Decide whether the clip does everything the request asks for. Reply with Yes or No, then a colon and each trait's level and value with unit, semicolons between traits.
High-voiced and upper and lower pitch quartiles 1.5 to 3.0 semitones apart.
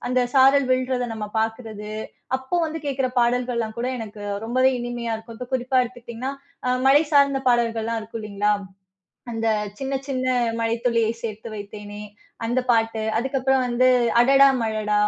Yes: high, 240 Hz; narrow, 2.5 semitones